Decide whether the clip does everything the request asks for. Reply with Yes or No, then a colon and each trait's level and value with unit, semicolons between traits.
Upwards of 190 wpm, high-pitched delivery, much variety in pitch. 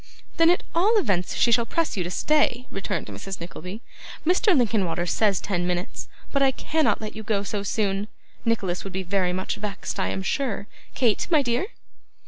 No: average, 185 wpm; high, 210 Hz; wide, 5.7 semitones